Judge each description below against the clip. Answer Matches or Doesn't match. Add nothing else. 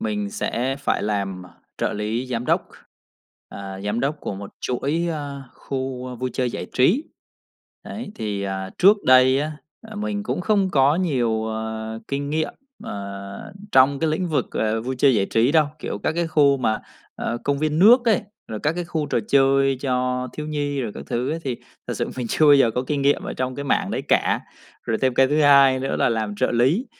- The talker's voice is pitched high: Doesn't match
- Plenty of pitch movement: Doesn't match